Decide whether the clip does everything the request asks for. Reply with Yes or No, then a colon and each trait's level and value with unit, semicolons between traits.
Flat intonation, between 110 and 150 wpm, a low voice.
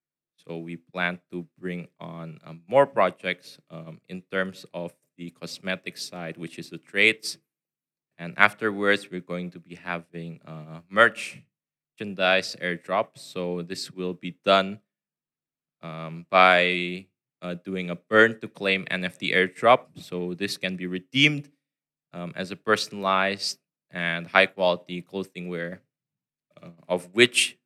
Yes: narrow, 2.1 semitones; slow, 135 wpm; very low, 90 Hz